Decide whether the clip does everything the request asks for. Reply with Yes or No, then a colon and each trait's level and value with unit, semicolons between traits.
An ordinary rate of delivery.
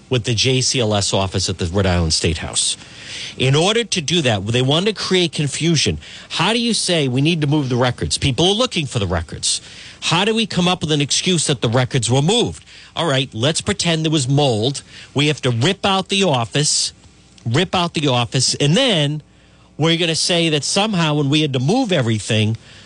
No: fast, 210 wpm